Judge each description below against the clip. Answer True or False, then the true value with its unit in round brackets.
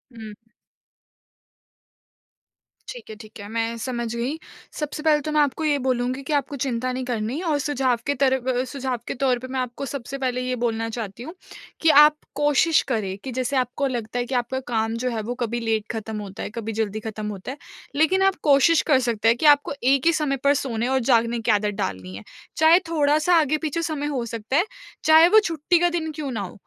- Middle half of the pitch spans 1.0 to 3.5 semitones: False (4.4 semitones)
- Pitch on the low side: False (255 Hz)